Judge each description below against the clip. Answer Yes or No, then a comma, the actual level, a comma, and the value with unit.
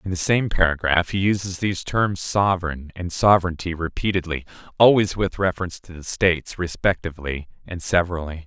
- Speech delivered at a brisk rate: No, average, 140 wpm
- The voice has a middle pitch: No, very low, 90 Hz